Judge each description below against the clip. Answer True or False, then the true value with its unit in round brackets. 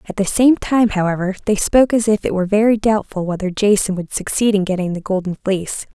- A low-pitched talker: False (200 Hz)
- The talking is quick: True (220 wpm)